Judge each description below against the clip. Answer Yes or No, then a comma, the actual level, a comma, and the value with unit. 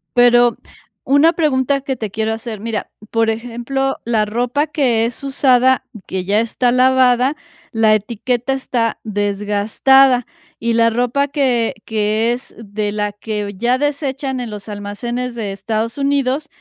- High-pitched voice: Yes, high, 235 Hz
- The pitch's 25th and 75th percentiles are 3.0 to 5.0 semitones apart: Yes, average, 3.3 semitones